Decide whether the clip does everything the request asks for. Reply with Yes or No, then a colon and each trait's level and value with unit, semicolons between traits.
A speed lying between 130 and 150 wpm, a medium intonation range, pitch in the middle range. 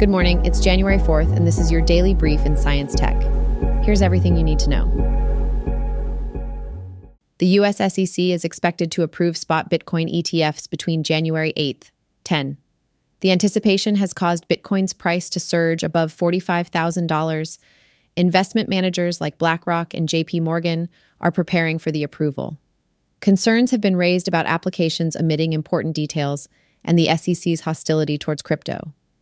No: average, 145 wpm; narrow, 2.3 semitones; medium, 165 Hz